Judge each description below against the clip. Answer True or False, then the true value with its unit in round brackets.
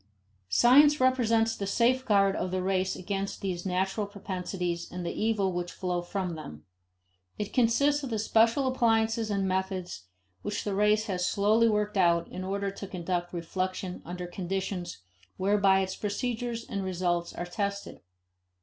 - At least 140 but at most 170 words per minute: True (150 wpm)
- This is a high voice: True (195 Hz)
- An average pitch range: True (3.4 semitones)